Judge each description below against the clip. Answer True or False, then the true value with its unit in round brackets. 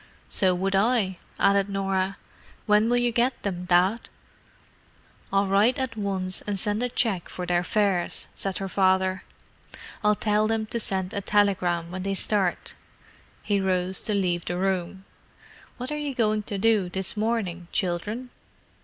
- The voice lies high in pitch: True (195 Hz)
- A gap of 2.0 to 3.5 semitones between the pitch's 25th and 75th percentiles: True (2.5 semitones)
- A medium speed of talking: True (160 wpm)